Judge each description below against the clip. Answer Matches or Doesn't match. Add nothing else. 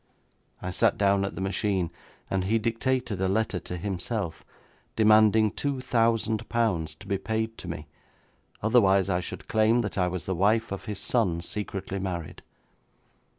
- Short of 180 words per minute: Matches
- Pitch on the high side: Doesn't match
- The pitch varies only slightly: Doesn't match